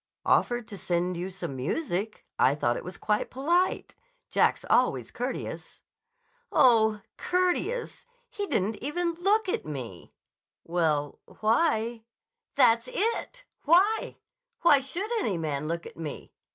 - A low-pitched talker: No, high, 225 Hz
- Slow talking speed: Yes, slow, 125 wpm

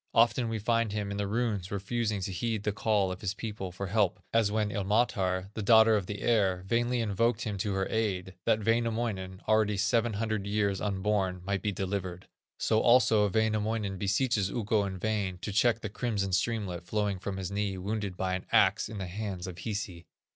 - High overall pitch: No, low, 105 Hz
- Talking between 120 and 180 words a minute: No, average, 195 wpm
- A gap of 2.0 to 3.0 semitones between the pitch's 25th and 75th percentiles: Yes, narrow, 2.5 semitones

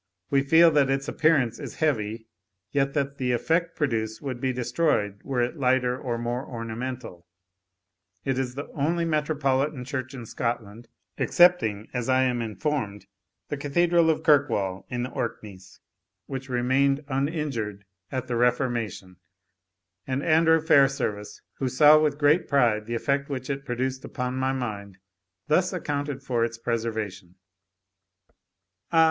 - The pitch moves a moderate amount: Yes, average, 3.7 semitones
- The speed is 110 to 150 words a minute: Yes, average, 140 wpm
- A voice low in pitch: Yes, low, 130 Hz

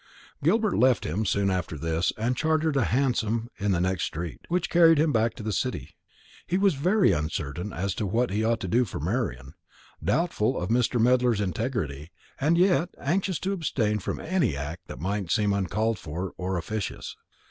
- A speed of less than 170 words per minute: No, average, 185 wpm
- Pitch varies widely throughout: Yes, wide, 7.2 semitones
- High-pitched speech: No, low, 110 Hz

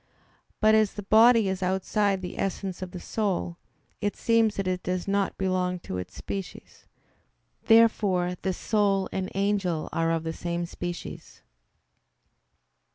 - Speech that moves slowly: No, average, 145 wpm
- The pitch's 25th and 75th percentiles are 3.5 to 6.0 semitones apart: No, narrow, 2.4 semitones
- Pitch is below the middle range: No, high, 190 Hz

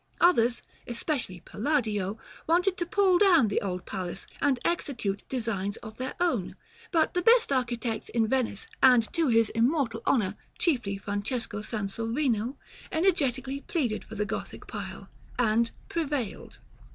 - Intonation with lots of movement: Yes, wide, 5.8 semitones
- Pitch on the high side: Yes, high, 240 Hz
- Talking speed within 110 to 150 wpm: Yes, slow, 135 wpm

